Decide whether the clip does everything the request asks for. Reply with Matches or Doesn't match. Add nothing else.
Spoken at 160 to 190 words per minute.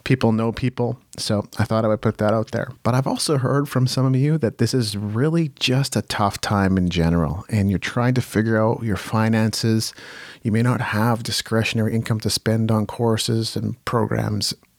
Doesn't match